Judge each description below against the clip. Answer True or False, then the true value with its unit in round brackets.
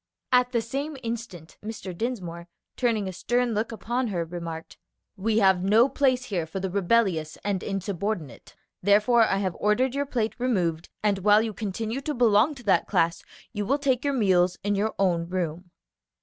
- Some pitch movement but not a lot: True (4.7 semitones)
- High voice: True (210 Hz)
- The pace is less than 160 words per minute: False (180 wpm)